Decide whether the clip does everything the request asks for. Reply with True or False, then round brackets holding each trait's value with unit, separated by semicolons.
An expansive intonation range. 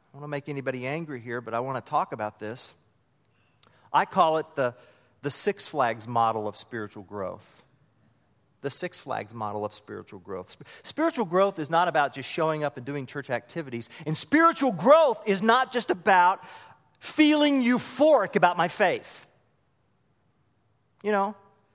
True (8.4 semitones)